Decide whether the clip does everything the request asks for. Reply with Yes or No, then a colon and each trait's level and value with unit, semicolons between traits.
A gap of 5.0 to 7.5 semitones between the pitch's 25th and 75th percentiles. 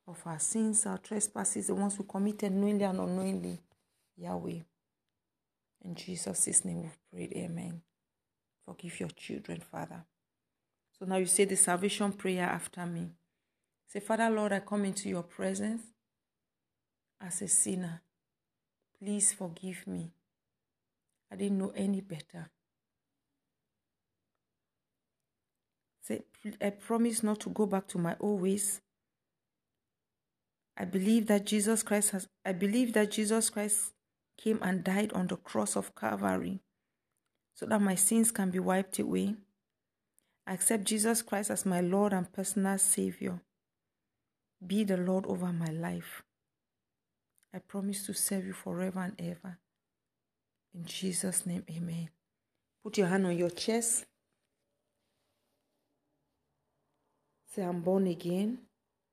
No: average, 2.8 semitones